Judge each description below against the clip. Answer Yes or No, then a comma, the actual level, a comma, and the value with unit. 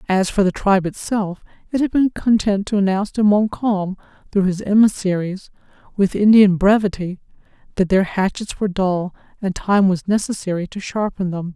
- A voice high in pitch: Yes, high, 195 Hz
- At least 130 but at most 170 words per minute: Yes, average, 160 wpm